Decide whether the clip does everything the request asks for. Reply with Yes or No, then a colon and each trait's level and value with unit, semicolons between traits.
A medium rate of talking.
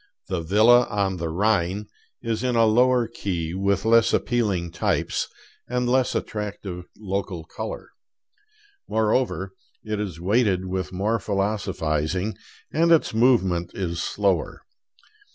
No: slow, 120 wpm